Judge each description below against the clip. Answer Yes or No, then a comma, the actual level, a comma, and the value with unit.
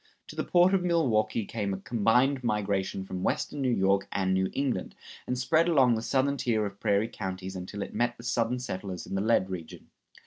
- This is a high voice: No, low, 110 Hz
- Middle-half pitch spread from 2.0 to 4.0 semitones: No, average, 4.8 semitones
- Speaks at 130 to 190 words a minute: No, fast, 205 wpm